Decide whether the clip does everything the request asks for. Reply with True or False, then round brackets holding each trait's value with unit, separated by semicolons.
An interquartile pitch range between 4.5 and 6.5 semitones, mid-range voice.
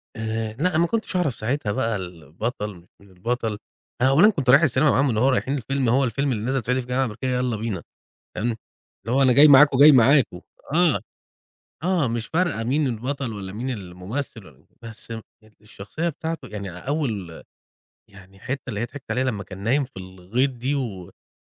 False (4.8 semitones; 125 Hz)